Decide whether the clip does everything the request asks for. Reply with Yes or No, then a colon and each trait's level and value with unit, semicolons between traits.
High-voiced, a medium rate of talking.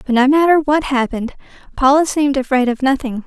Yes: very high, 270 Hz; average, 185 wpm